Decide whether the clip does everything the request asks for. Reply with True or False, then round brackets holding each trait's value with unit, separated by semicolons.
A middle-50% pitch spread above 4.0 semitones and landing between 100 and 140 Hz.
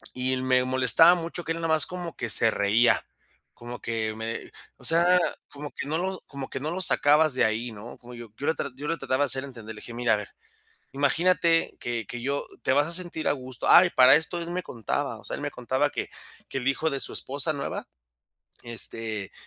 True (5.3 semitones; 135 Hz)